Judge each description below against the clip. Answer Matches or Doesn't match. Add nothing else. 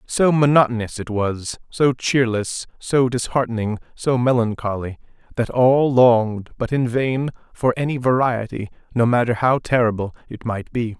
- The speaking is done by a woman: Doesn't match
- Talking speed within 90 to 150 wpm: Matches